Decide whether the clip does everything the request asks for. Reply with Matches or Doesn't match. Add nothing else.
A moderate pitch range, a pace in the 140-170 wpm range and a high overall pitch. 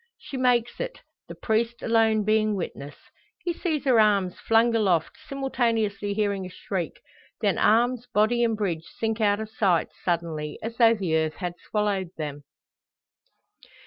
Matches